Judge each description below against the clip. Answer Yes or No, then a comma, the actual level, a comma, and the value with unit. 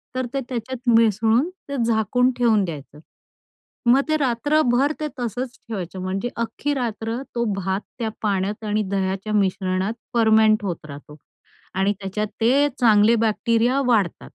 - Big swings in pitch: No, average, 3.8 semitones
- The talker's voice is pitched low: No, high, 225 Hz